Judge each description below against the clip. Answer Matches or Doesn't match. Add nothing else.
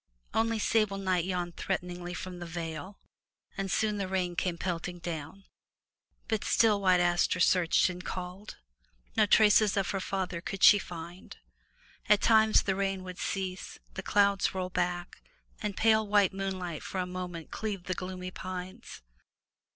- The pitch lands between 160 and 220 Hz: Matches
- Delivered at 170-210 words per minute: Doesn't match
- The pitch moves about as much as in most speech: Doesn't match